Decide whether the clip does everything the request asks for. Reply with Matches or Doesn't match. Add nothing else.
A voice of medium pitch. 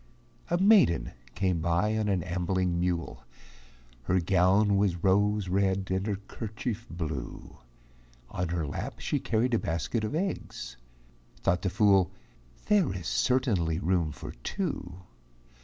Doesn't match